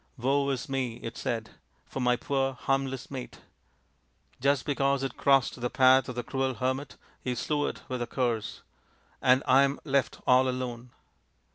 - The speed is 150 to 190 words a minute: Yes, average, 175 wpm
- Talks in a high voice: No, low, 130 Hz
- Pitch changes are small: Yes, narrow, 1.6 semitones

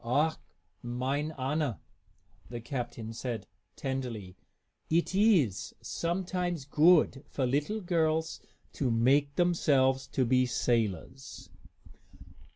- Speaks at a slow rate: Yes, slow, 95 wpm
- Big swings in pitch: No, average, 4.7 semitones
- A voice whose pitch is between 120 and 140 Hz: Yes, low, 135 Hz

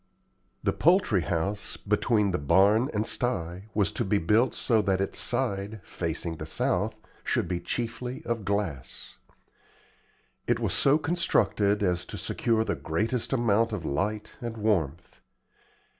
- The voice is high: No, low, 105 Hz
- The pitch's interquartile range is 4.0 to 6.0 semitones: Yes, average, 4.4 semitones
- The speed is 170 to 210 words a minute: No, average, 145 wpm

